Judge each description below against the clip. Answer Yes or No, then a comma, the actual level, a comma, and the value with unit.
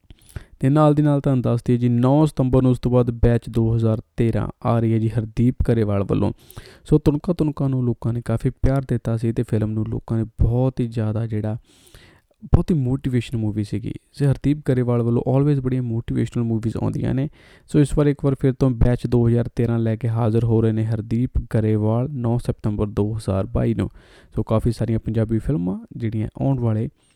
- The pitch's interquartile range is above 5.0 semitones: No, average, 2.8 semitones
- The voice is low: Yes, low, 120 Hz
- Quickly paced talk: Yes, fast, 190 wpm